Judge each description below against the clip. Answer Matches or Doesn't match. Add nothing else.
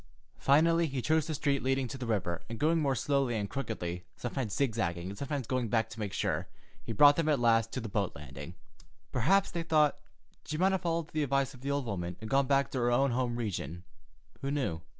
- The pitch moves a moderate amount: Matches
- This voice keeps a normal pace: Doesn't match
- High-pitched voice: Doesn't match